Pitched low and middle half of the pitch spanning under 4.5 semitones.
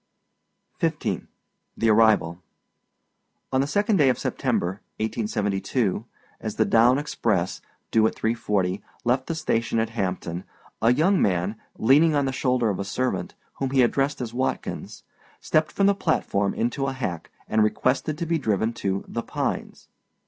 No: low, 115 Hz; average, 4.8 semitones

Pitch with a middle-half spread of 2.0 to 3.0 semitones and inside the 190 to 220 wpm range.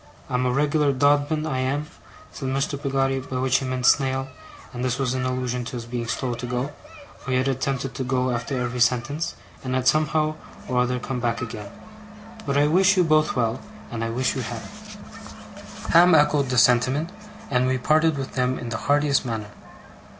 Yes: narrow, 2.6 semitones; average, 195 wpm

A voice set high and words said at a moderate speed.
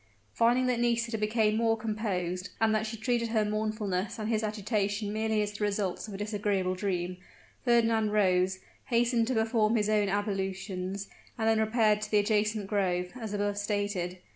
Yes: high, 210 Hz; average, 170 wpm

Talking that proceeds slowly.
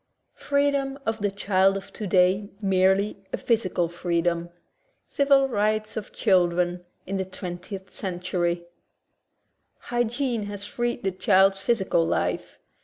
Yes: slow, 120 wpm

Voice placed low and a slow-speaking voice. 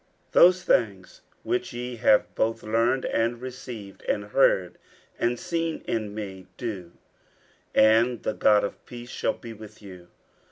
No: low, 115 Hz; average, 150 wpm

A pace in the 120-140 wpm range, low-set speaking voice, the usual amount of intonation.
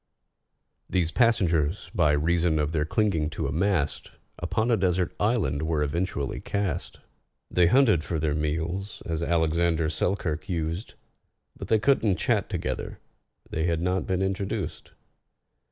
Yes: slow, 135 wpm; very low, 85 Hz; average, 3.6 semitones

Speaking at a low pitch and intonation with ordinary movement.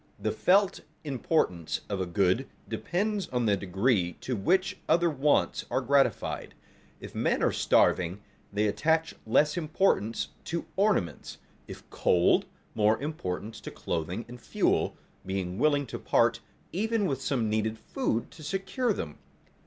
No: low, 125 Hz; wide, 8.9 semitones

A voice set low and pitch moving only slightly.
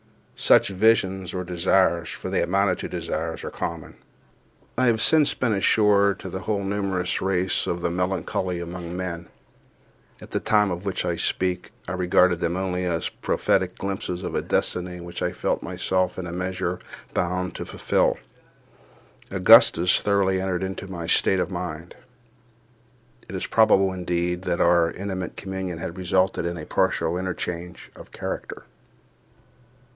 Yes: very low, 90 Hz; narrow, 1.6 semitones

